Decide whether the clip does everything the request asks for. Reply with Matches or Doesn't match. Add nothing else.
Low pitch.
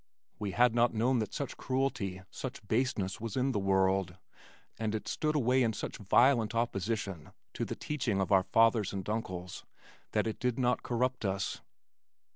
Matches